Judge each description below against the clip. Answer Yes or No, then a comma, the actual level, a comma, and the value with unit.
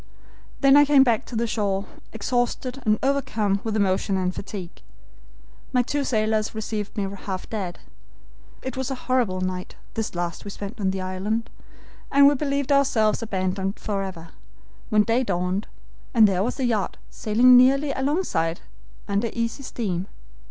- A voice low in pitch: No, high, 215 Hz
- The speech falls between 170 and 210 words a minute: No, average, 155 wpm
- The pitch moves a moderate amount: Yes, average, 4.8 semitones